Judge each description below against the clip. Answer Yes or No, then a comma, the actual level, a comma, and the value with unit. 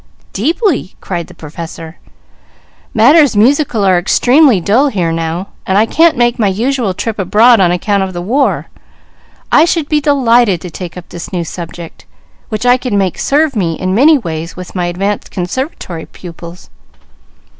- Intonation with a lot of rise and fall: Yes, wide, 6.4 semitones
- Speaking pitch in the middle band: No, high, 200 Hz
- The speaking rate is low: No, average, 165 wpm